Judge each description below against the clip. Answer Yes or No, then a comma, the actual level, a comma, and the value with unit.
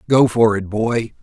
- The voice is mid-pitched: No, low, 110 Hz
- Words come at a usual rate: Yes, average, 195 wpm